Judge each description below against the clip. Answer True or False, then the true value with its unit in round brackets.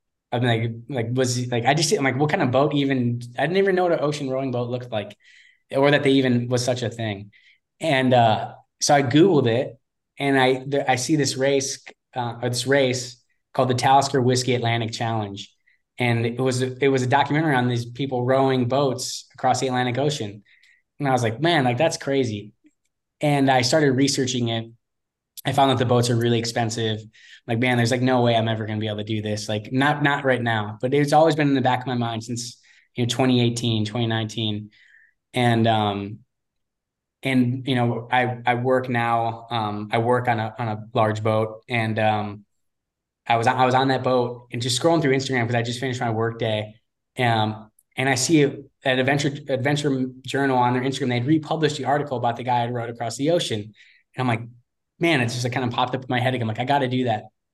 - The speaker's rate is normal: False (220 wpm)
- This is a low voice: True (125 Hz)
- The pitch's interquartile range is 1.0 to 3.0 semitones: True (2.6 semitones)